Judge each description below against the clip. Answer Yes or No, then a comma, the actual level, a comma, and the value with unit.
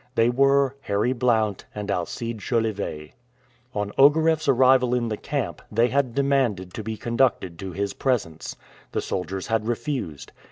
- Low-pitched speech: Yes, low, 115 Hz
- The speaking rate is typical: Yes, average, 150 wpm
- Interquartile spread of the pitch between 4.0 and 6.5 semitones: Yes, average, 4.6 semitones